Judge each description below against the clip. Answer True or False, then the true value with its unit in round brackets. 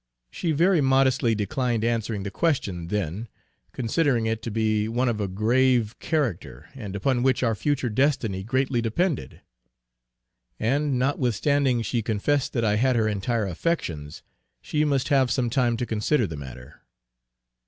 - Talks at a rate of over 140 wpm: True (150 wpm)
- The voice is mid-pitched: False (120 Hz)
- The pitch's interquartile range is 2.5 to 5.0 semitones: True (4.1 semitones)